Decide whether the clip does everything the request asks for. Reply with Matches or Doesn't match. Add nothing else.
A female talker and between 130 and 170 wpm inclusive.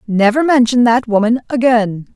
Matches